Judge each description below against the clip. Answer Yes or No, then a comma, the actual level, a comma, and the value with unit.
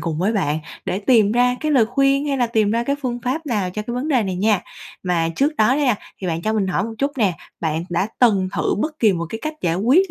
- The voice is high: Yes, high, 225 Hz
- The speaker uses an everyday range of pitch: No, wide, 5.9 semitones